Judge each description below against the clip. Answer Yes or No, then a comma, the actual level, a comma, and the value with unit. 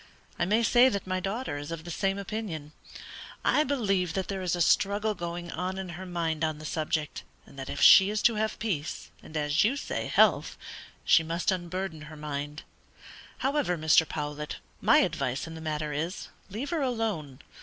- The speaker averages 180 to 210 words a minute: Yes, average, 190 wpm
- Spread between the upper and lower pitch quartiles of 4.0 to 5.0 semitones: Yes, average, 4.7 semitones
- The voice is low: No, medium, 175 Hz